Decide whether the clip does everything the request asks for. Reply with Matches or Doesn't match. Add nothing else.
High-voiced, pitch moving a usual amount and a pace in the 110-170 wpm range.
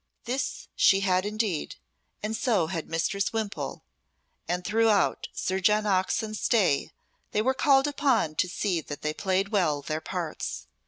Matches